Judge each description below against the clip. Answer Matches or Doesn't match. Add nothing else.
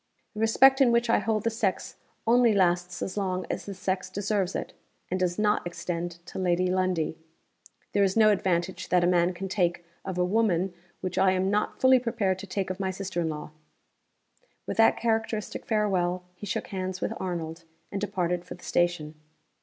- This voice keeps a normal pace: Matches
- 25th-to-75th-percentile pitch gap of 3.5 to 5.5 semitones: Doesn't match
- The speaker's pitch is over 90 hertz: Matches